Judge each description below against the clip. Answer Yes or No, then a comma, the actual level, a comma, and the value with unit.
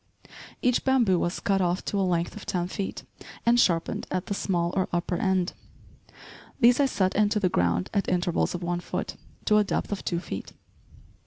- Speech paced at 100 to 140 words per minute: No, average, 190 wpm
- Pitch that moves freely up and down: No, average, 2.9 semitones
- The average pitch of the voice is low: No, medium, 185 Hz